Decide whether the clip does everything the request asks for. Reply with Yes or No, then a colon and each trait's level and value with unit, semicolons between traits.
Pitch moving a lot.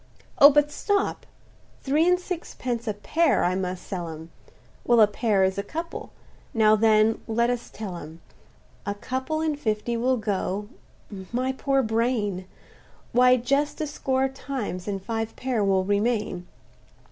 No: average, 4.7 semitones